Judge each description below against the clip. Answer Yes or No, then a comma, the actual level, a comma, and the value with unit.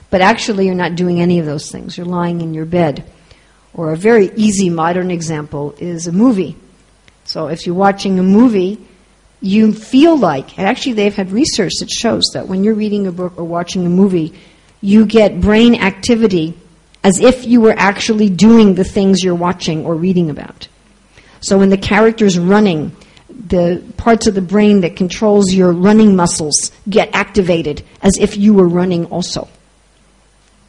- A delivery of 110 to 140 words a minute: No, average, 175 wpm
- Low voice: No, high, 190 Hz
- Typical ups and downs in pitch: Yes, average, 3.3 semitones